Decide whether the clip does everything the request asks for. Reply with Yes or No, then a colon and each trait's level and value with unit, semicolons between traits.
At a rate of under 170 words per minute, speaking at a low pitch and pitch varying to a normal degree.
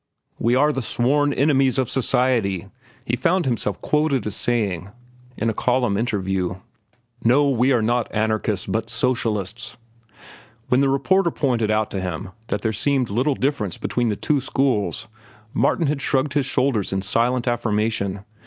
Yes: average, 155 wpm; low, 120 Hz; average, 4.2 semitones